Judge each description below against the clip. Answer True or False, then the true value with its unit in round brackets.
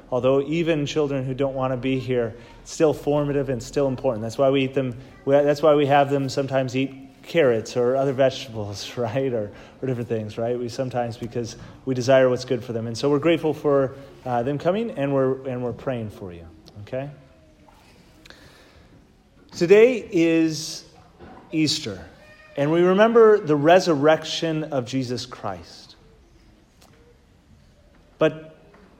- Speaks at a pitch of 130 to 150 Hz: True (135 Hz)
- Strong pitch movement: False (3.7 semitones)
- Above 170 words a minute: False (155 wpm)